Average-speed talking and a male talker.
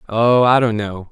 No: fast, 215 wpm; male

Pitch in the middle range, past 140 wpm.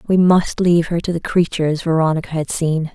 Yes: medium, 165 Hz; fast, 205 wpm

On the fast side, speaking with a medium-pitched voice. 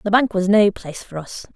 No: fast, 270 wpm; high, 200 Hz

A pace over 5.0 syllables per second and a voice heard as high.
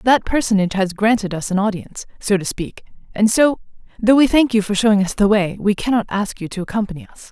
Yes: 6.1 syllables/s; high, 210 Hz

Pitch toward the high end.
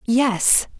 Yes: high, 225 Hz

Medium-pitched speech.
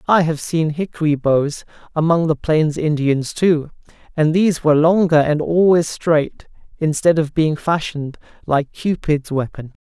Yes: medium, 155 Hz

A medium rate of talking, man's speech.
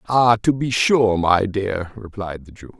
Yes: average, 195 wpm; male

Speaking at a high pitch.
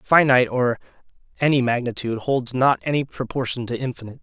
No: low, 125 Hz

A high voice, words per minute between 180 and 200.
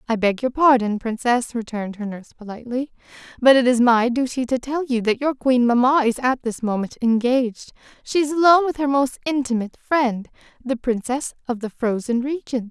Yes: high, 245 Hz; average, 190 wpm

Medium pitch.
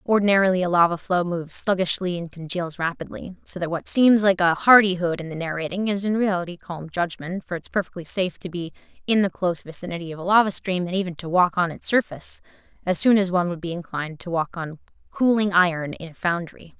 Yes: medium, 180 Hz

